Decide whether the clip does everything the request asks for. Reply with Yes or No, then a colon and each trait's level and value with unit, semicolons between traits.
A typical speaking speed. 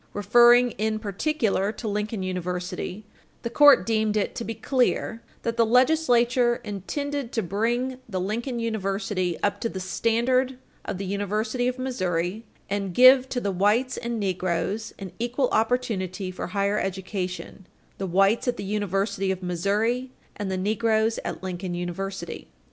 Yes: average, 150 wpm